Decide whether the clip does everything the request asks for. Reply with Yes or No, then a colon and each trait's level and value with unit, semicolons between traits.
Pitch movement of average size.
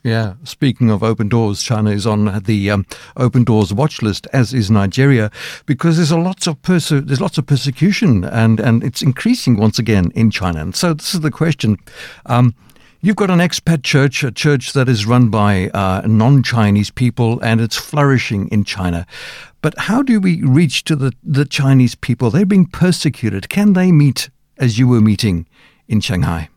No: wide, 5.8 semitones